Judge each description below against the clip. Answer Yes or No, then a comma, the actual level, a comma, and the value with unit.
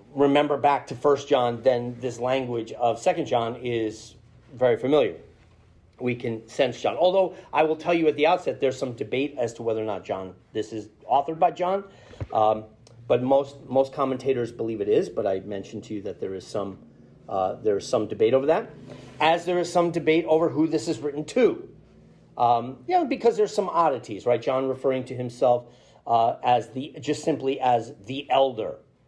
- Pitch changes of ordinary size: Yes, average, 4.6 semitones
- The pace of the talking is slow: No, average, 195 wpm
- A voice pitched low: Yes, low, 130 Hz